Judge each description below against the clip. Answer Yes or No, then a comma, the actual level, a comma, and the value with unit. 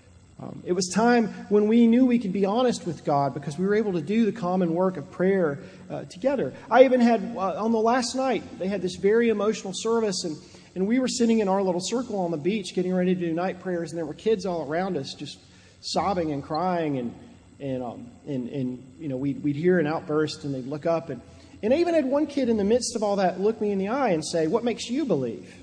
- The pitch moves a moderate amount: No, wide, 5.7 semitones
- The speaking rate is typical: No, fast, 260 wpm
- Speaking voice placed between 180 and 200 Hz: Yes, high, 190 Hz